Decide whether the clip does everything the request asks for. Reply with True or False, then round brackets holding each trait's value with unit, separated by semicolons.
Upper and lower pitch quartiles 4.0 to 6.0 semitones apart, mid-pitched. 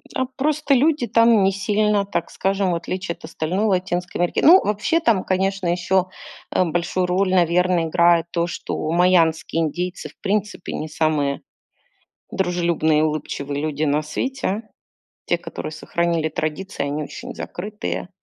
False (3.4 semitones; 180 Hz)